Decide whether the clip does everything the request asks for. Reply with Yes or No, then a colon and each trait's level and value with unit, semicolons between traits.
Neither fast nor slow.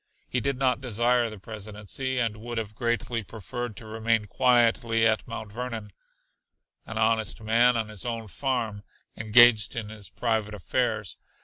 Yes: average, 150 wpm